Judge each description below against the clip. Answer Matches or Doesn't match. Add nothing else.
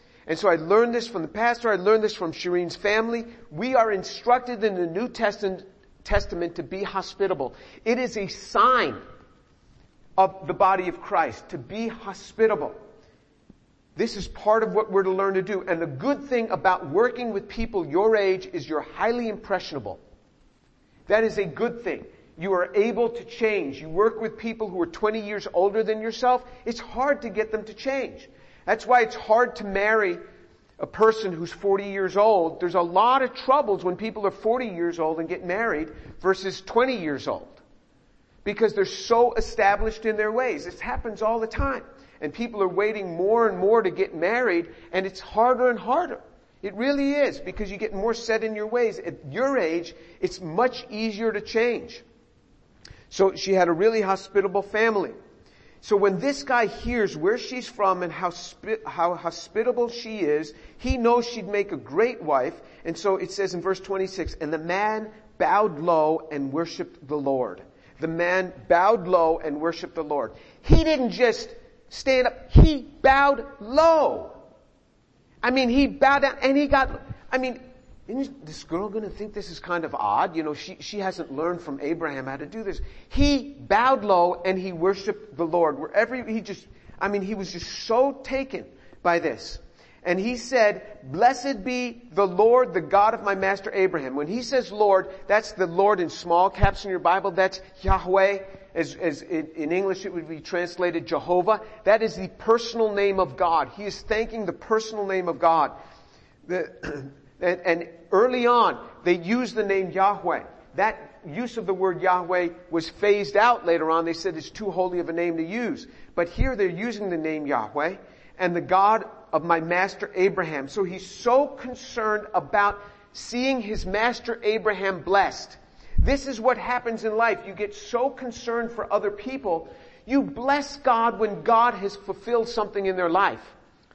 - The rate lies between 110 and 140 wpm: Doesn't match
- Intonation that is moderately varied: Matches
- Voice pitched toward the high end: Matches